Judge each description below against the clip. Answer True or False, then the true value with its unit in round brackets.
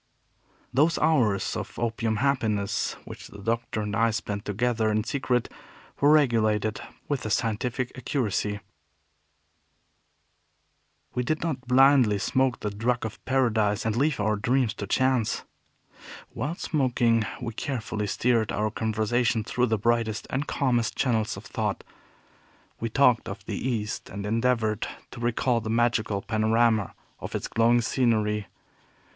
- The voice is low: True (115 Hz)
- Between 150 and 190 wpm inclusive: False (135 wpm)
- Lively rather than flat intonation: False (2.8 semitones)